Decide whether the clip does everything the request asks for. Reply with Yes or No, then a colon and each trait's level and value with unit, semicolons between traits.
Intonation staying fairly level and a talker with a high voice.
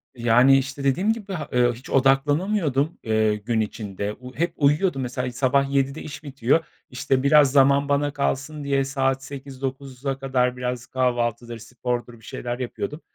No: narrow, 2.3 semitones; low, 135 Hz